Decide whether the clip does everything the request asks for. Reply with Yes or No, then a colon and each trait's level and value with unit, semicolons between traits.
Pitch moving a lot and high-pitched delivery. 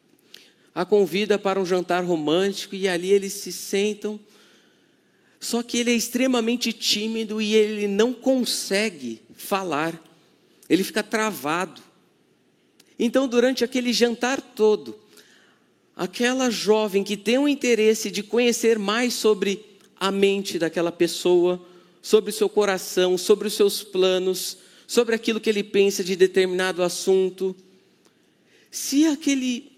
No: average, 3.7 semitones; high, 205 Hz